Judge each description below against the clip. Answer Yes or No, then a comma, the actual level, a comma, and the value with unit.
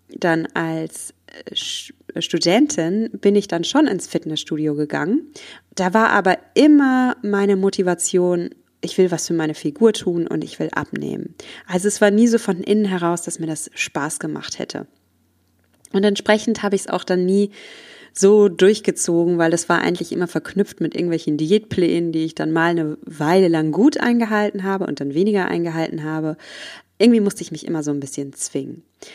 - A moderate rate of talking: Yes, average, 175 wpm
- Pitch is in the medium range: Yes, medium, 180 Hz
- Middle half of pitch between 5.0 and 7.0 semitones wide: No, average, 4.2 semitones